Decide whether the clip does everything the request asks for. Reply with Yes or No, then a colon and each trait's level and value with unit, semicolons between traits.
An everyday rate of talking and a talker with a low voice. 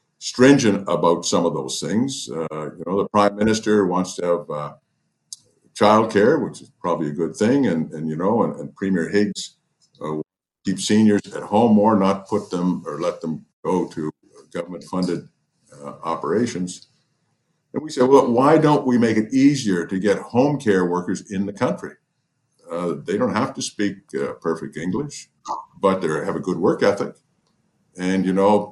Yes: average, 180 wpm; low, 100 Hz